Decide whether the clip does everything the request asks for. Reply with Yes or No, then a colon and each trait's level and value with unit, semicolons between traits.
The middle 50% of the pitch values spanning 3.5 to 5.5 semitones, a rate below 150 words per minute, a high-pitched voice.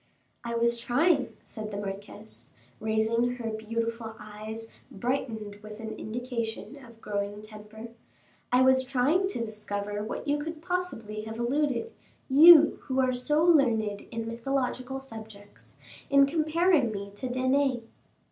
Yes: average, 3.9 semitones; average, 140 wpm; high, 235 Hz